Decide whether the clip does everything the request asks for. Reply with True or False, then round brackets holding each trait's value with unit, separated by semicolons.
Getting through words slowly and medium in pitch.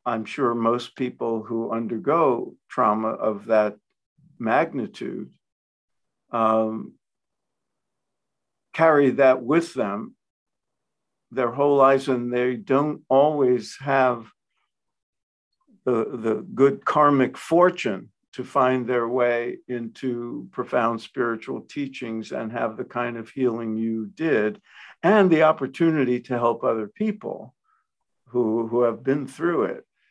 False (115 wpm; 125 Hz)